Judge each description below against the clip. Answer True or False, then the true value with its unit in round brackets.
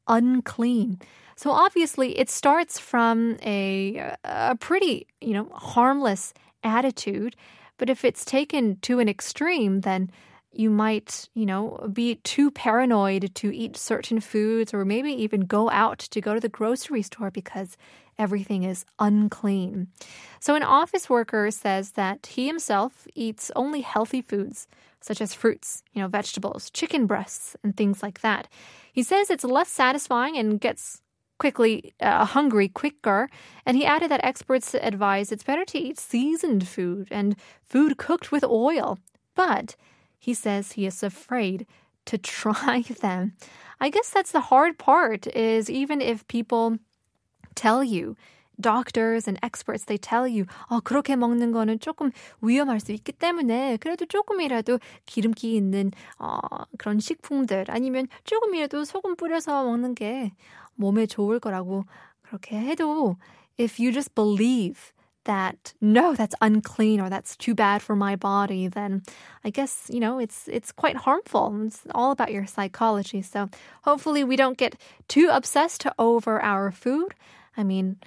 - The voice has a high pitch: True (230 Hz)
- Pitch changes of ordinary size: True (4.4 semitones)